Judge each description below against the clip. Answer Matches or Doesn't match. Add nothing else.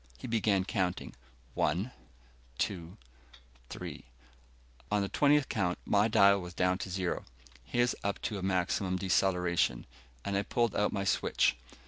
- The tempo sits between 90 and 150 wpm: Matches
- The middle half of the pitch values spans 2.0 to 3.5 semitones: Matches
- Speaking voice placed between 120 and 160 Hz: Doesn't match